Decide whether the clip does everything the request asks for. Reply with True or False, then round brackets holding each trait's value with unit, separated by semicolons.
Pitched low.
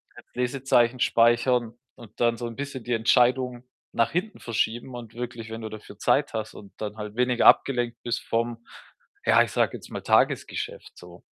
True (120 Hz)